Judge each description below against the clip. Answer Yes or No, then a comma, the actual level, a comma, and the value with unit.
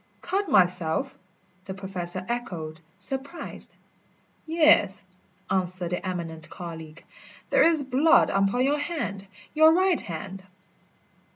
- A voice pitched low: No, high, 195 Hz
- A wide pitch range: Yes, wide, 9.0 semitones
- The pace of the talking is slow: Yes, slow, 105 wpm